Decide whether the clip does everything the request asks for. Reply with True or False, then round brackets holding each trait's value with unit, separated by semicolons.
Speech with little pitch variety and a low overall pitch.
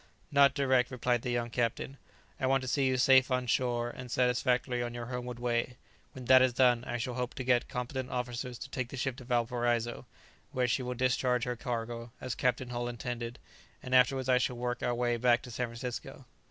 True (1.2 semitones; 125 Hz)